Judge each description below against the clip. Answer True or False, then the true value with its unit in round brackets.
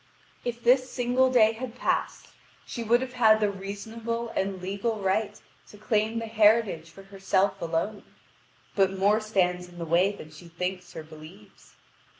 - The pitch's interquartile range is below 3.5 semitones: False (3.8 semitones)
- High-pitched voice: True (205 Hz)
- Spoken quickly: False (160 wpm)